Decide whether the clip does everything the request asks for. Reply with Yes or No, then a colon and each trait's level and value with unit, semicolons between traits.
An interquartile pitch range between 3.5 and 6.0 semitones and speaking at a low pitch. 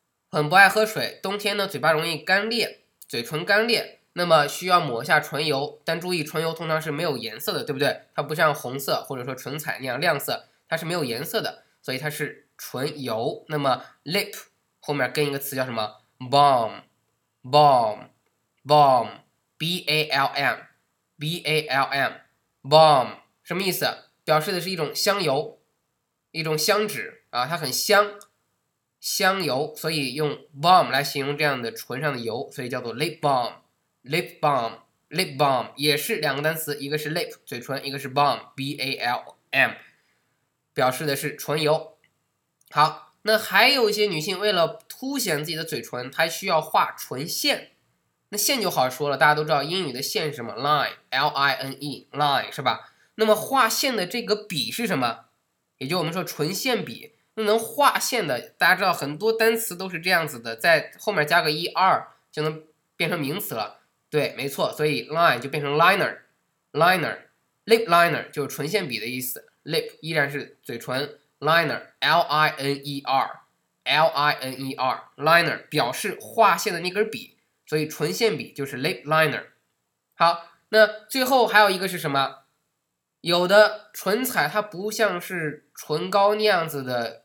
No: average, 5.2 semitones; medium, 155 Hz